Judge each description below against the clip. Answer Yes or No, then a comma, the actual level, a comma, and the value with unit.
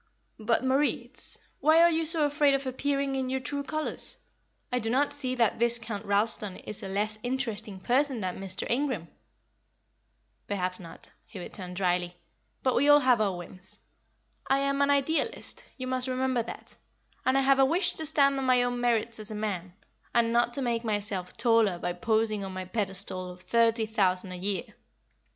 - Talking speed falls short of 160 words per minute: No, average, 180 wpm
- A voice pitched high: Yes, high, 230 Hz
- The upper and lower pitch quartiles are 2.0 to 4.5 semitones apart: No, average, 5.1 semitones